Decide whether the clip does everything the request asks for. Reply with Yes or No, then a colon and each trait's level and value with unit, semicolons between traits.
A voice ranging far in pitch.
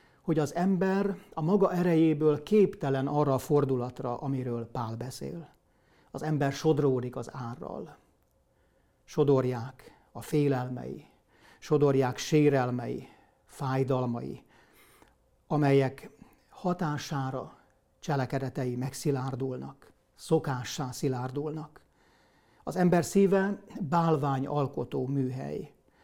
No: average, 3.8 semitones